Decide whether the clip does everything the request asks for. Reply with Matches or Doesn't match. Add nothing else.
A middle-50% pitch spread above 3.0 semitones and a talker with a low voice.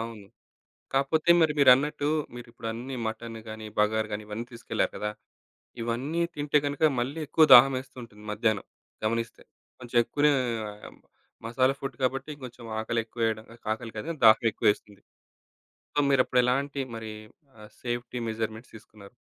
Matches